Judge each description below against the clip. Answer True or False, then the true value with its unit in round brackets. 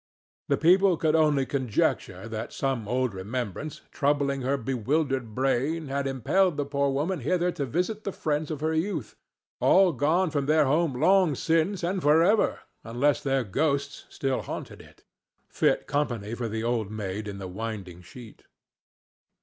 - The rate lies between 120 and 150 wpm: False (160 wpm)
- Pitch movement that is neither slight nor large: True (5.0 semitones)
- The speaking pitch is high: False (140 Hz)